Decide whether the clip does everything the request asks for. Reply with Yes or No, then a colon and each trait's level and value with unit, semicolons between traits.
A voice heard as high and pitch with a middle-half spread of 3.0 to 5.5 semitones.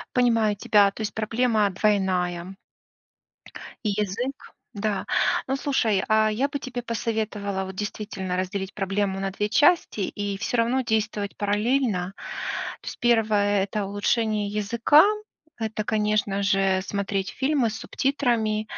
No: high, 210 Hz; narrow, 2.5 semitones